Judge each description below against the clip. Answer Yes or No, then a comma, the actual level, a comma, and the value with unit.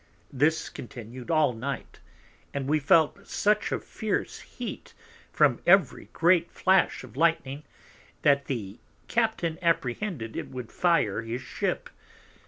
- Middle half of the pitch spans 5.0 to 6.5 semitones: Yes, average, 5.3 semitones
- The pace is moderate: No, slow, 125 wpm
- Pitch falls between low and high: Yes, medium, 145 Hz